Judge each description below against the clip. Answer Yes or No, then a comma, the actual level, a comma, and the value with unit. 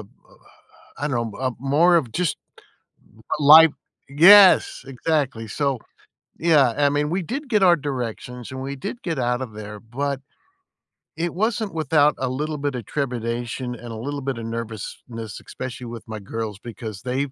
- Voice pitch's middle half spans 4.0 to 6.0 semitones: Yes, average, 4.5 semitones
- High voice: No, low, 135 Hz